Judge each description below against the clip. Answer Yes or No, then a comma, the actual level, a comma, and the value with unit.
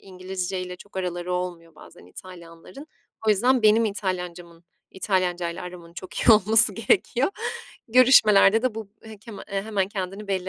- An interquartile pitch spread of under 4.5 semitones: Yes, average, 3.2 semitones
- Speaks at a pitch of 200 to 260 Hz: No, high, 190 Hz